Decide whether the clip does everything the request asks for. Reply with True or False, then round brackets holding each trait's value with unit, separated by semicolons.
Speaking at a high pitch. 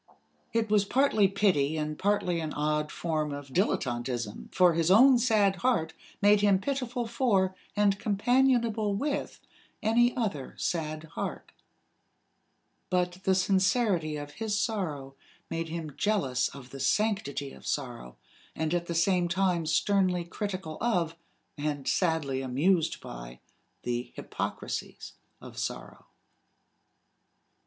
False (180 Hz)